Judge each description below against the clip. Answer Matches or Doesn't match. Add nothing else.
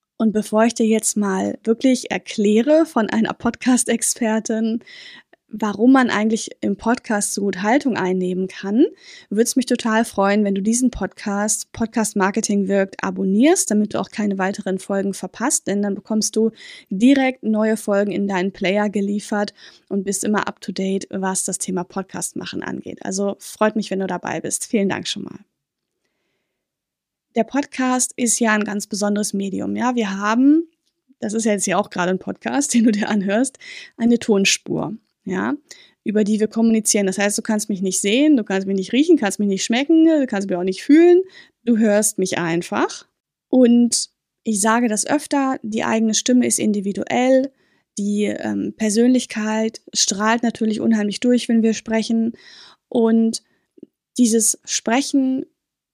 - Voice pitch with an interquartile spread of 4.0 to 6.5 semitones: Doesn't match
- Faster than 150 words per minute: Matches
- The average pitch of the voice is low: Doesn't match